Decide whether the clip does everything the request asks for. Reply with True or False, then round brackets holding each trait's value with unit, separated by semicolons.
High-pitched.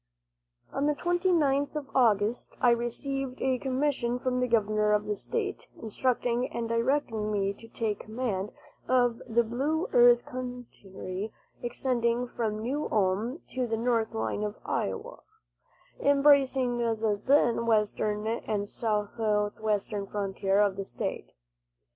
True (235 Hz)